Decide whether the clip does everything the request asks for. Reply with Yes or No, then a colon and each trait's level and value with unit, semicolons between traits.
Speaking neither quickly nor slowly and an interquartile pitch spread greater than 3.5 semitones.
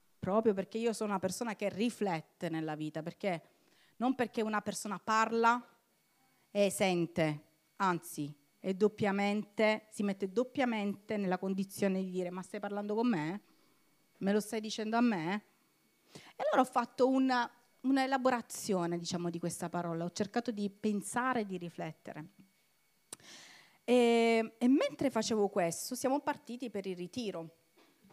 Yes: average, 135 wpm; average, 4.3 semitones